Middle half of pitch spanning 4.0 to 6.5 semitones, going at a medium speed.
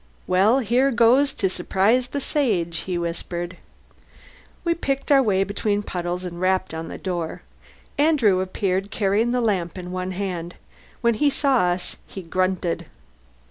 Yes: average, 5.0 semitones; average, 150 wpm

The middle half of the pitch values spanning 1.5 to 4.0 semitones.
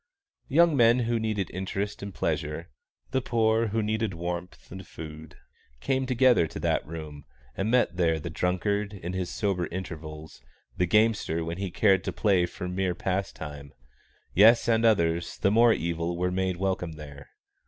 No: average, 4.7 semitones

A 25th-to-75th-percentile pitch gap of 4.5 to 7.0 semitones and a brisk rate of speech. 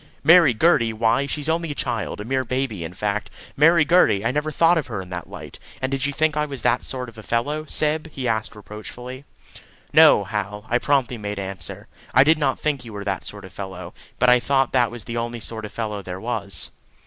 Yes: average, 5.3 semitones; fast, 230 wpm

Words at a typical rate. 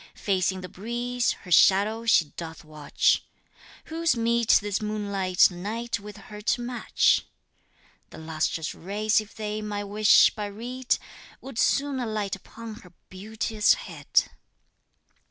No: slow, 130 wpm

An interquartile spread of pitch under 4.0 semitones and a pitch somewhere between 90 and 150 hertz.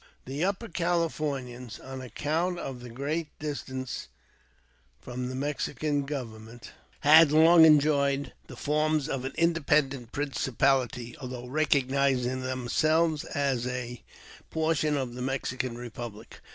Yes: average, 3.4 semitones; low, 135 Hz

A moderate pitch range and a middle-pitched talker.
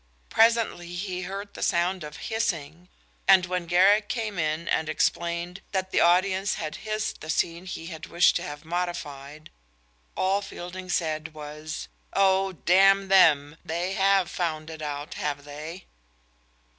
Yes: average, 3.4 semitones; medium, 175 Hz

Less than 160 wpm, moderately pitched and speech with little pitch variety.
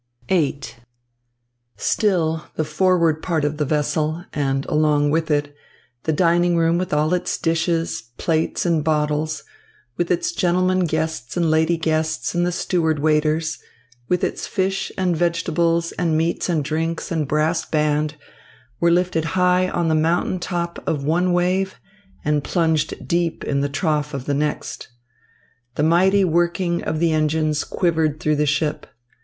Yes: average, 150 wpm; medium, 160 Hz; narrow, 2.3 semitones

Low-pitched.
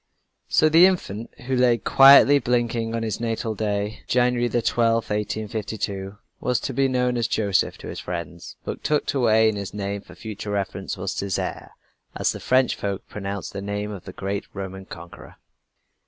Yes: low, 110 Hz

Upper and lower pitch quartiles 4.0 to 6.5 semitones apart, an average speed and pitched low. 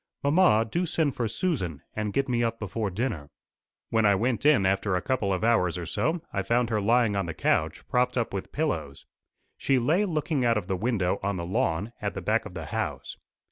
No: average, 5.1 semitones; fast, 220 wpm; low, 115 Hz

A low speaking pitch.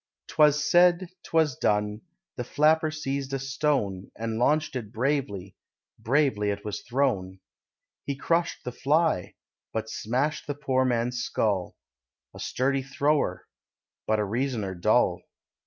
Yes: low, 130 Hz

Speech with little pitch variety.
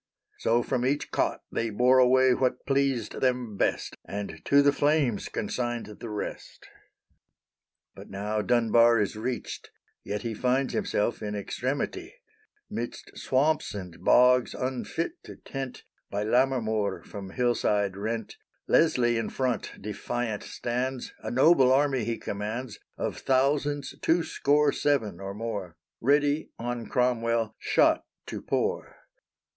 No: average, 3.7 semitones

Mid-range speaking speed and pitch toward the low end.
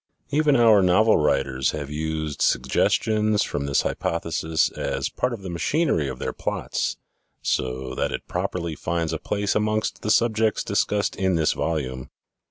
Yes: average, 155 wpm; very low, 85 Hz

